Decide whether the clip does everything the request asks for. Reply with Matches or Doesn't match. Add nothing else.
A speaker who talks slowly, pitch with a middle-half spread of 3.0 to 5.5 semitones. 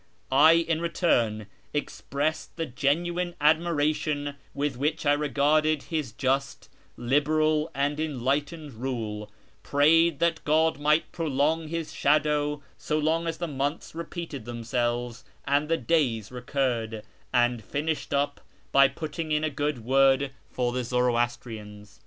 Matches